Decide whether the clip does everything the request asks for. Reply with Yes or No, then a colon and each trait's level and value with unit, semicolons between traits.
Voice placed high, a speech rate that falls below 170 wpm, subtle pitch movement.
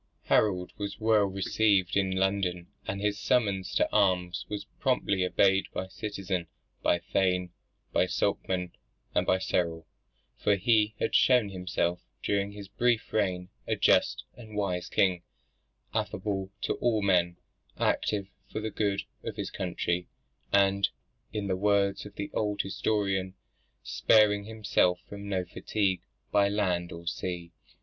No: low, 100 Hz; average, 140 wpm; narrow, 2.2 semitones